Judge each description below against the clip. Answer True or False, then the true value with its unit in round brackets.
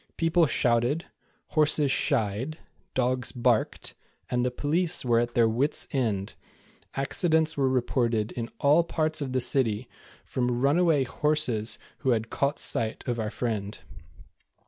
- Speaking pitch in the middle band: False (130 Hz)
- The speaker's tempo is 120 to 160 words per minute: True (135 wpm)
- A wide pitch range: False (4.2 semitones)